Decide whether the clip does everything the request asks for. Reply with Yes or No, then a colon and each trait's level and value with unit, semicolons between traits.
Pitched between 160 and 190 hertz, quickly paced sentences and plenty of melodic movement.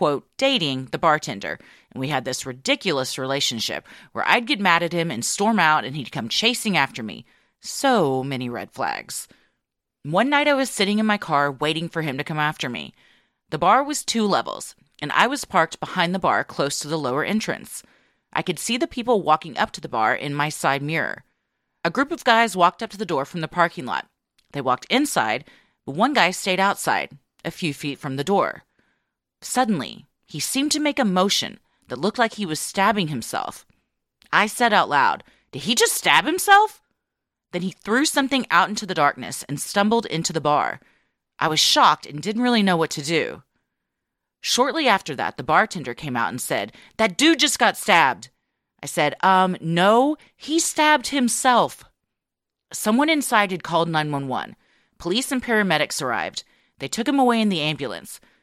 No: medium, 185 Hz; average, 190 wpm; wide, 7.8 semitones